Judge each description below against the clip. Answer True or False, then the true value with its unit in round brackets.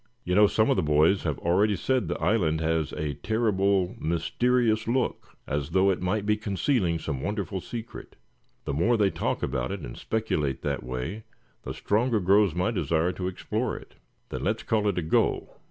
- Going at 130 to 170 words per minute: False (185 wpm)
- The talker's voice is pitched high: False (95 Hz)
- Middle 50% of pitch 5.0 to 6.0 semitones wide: True (5.3 semitones)